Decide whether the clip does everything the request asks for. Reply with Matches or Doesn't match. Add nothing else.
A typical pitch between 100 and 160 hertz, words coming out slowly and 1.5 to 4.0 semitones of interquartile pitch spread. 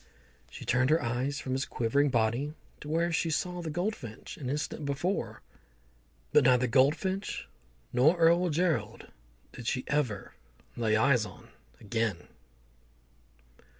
Doesn't match